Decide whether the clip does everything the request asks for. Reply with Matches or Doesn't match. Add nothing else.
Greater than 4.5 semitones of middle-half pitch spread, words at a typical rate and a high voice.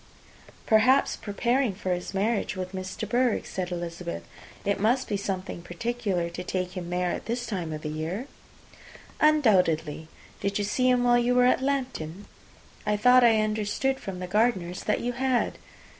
Matches